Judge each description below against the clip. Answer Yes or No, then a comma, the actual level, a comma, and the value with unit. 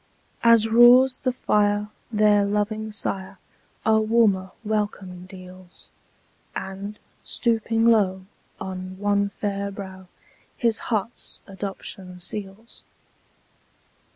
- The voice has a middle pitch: No, high, 205 Hz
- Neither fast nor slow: No, slow, 95 wpm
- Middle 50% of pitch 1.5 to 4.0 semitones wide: Yes, narrow, 2.5 semitones